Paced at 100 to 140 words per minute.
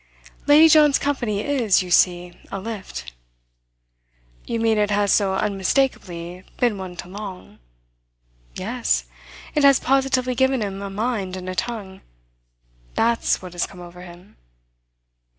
Yes: slow, 135 wpm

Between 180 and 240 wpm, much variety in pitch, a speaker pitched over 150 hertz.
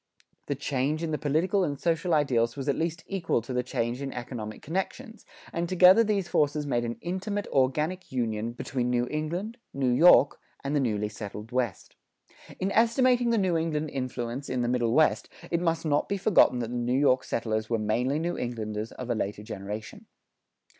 No: average, 190 wpm; wide, 6.0 semitones; medium, 140 Hz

